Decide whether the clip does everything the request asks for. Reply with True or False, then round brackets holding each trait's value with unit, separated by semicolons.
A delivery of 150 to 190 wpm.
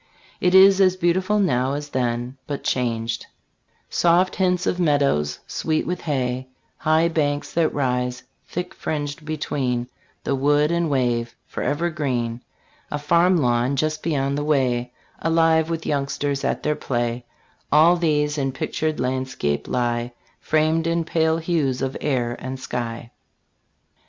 False (140 wpm)